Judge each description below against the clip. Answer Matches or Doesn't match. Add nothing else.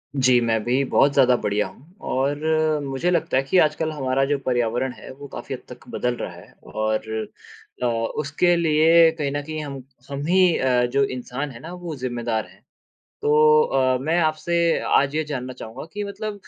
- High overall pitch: Doesn't match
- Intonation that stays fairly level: Doesn't match